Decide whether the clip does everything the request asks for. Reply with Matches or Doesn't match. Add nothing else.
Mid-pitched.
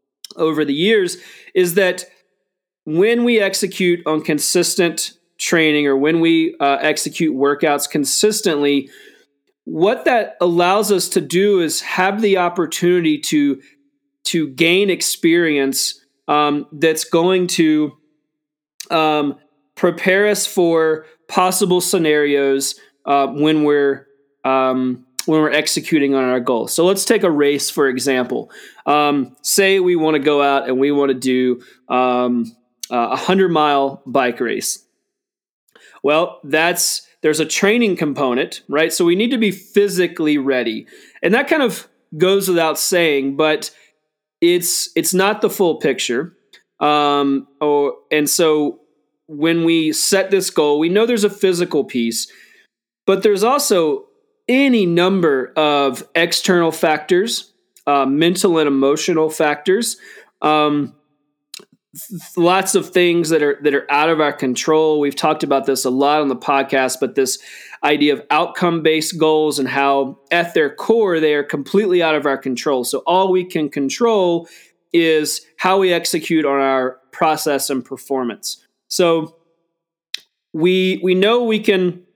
Matches